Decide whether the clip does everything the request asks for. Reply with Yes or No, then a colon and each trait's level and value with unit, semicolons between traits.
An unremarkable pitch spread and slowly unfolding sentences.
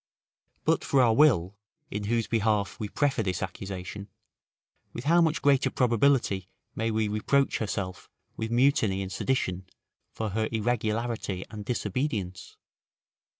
Yes: average, 4.1 semitones; slow, 130 wpm